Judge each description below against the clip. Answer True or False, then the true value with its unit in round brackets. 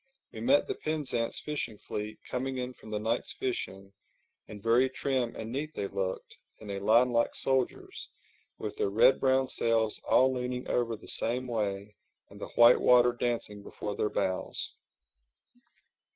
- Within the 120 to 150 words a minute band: False (160 wpm)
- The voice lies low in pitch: True (120 Hz)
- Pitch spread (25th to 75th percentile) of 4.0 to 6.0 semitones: False (3.6 semitones)